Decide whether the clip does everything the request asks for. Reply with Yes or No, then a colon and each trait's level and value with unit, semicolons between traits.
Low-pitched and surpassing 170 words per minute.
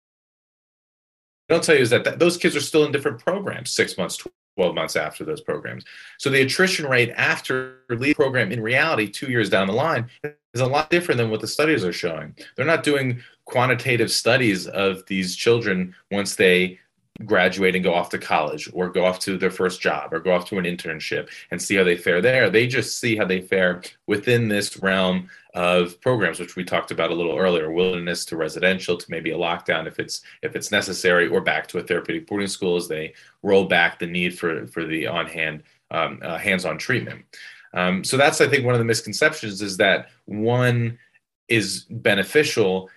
Yes: low, 100 Hz; average, 200 wpm